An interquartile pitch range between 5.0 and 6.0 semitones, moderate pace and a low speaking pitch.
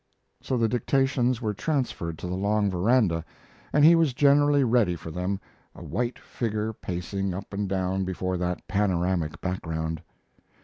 Yes: wide, 5.4 semitones; average, 150 wpm; low, 100 Hz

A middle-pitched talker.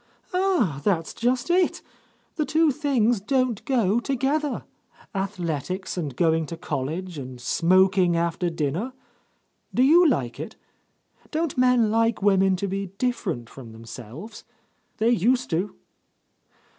No: high, 195 Hz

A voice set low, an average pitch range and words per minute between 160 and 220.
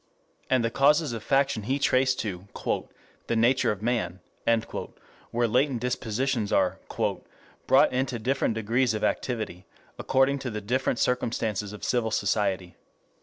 No: low, 120 Hz; average, 3.4 semitones; slow, 135 wpm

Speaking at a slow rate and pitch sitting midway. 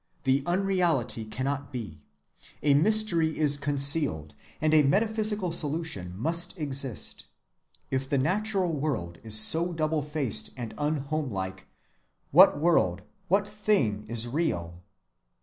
Yes: slow, 115 wpm; medium, 145 Hz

